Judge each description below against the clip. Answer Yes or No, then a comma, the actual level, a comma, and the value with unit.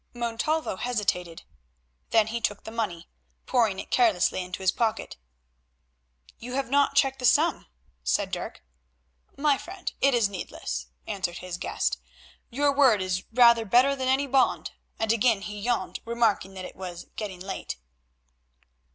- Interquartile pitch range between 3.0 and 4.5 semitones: No, wide, 5.4 semitones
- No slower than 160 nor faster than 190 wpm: No, average, 150 wpm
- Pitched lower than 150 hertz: No, high, 230 Hz